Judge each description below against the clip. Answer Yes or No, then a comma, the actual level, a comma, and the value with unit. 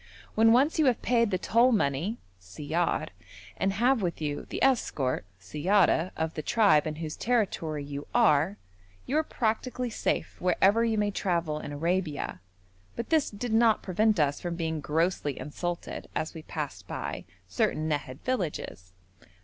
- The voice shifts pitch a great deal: Yes, wide, 6.8 semitones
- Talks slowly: No, average, 155 wpm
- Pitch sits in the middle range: Yes, medium, 175 Hz